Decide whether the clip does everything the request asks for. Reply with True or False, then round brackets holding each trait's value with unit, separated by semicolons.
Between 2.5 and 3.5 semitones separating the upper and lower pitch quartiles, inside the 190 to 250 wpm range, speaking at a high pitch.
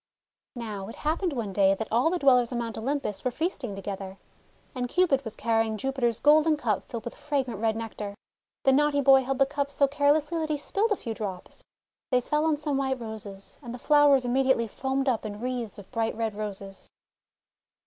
False (4.5 semitones; 200 wpm; 250 Hz)